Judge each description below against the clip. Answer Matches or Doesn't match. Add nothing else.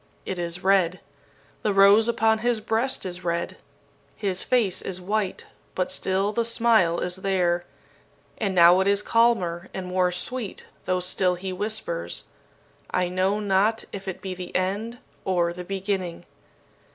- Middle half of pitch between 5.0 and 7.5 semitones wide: Doesn't match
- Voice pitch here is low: Doesn't match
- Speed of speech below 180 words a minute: Matches